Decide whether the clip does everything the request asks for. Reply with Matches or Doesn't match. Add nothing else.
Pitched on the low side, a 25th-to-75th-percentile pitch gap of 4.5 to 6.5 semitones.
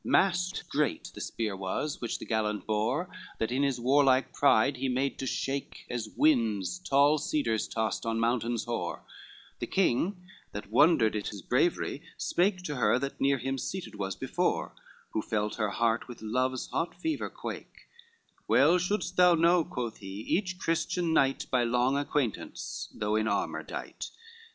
Matches